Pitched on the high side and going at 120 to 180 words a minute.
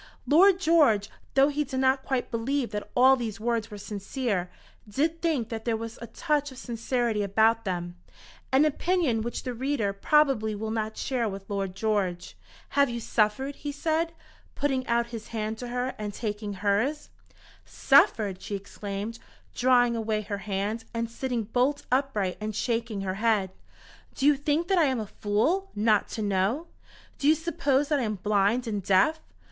Yes: high, 230 Hz; average, 175 wpm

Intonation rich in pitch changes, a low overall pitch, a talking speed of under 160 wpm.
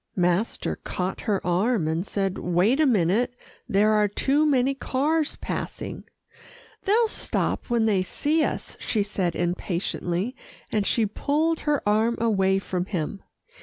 No: wide, 5.9 semitones; high, 210 Hz; average, 140 wpm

